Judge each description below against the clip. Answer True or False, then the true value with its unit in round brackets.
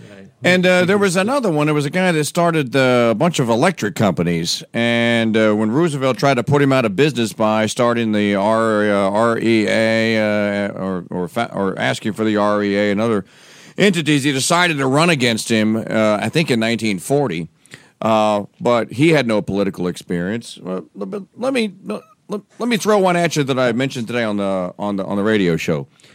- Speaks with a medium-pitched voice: False (115 Hz)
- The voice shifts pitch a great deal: True (6.4 semitones)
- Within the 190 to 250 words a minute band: True (200 wpm)